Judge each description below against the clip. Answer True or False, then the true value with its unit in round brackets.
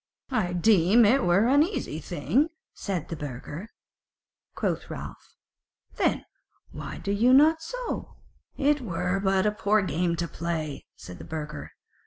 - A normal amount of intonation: False (6.9 semitones)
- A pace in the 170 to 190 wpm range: False (145 wpm)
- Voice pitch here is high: True (195 Hz)